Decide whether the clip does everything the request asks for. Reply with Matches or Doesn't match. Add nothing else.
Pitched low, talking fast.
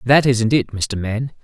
Matches